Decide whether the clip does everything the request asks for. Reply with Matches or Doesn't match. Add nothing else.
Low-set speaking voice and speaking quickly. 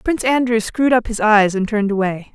Doesn't match